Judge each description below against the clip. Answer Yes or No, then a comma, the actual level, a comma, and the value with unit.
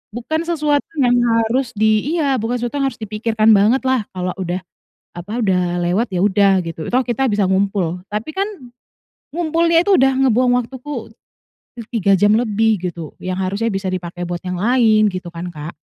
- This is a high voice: Yes, high, 215 Hz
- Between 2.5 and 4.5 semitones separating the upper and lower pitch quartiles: No, wide, 5.5 semitones